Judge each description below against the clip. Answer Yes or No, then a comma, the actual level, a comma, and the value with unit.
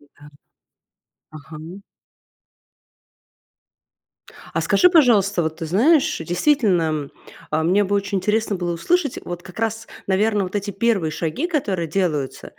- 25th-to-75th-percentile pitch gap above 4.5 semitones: Yes, average, 5.3 semitones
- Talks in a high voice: Yes, high, 195 Hz